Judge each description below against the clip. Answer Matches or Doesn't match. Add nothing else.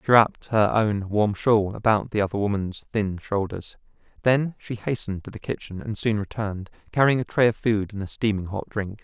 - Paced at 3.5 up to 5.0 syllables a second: Doesn't match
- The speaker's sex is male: Matches